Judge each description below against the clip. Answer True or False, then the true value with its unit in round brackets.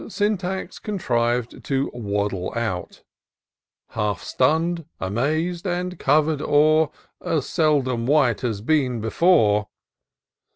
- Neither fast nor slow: False (95 wpm)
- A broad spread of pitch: True (6.2 semitones)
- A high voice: False (140 Hz)